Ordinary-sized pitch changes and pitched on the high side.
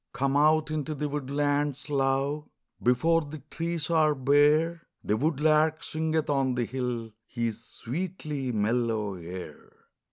No: average, 3.9 semitones; medium, 145 Hz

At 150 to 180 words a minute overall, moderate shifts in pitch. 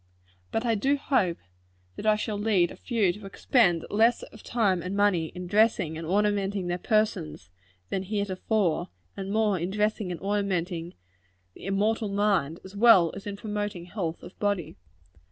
Yes: average, 170 wpm; average, 3.0 semitones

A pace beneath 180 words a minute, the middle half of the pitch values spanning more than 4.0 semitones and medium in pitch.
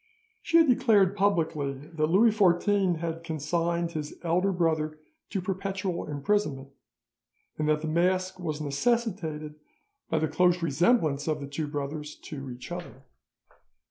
No: average, 140 wpm; average, 3.7 semitones; medium, 165 Hz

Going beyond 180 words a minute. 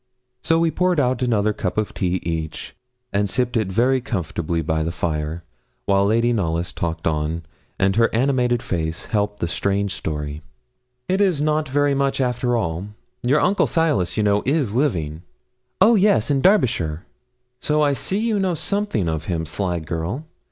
No: average, 175 wpm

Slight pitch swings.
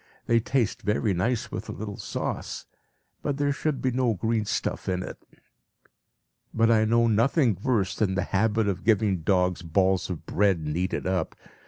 No: average, 3.9 semitones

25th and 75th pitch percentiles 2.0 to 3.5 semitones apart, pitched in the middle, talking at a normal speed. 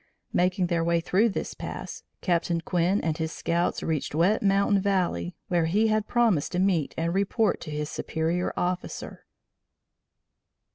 Yes: average, 3.1 semitones; medium, 175 Hz; average, 150 wpm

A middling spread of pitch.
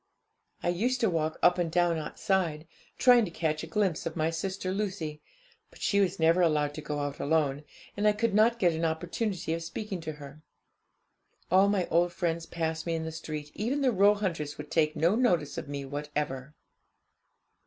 Yes: average, 4.1 semitones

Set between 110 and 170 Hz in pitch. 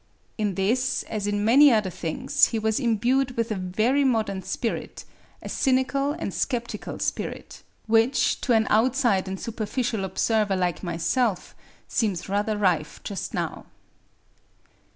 No: high, 220 Hz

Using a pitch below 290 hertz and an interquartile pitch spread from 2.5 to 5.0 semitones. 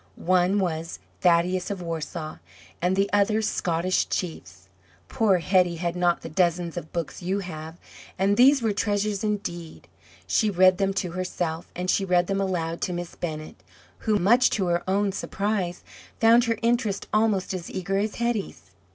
Yes: medium, 185 Hz; average, 3.0 semitones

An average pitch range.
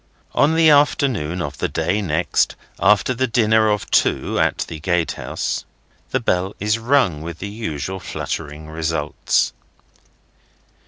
No: wide, 6.0 semitones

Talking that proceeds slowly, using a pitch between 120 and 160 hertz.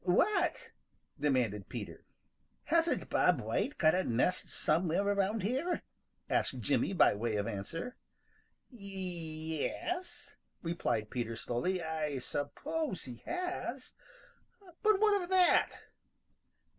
No: slow, 115 wpm; medium, 180 Hz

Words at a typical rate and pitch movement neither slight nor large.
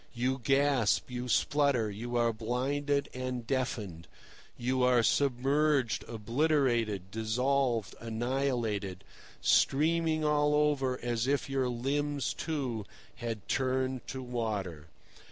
No: slow, 105 wpm; average, 3.4 semitones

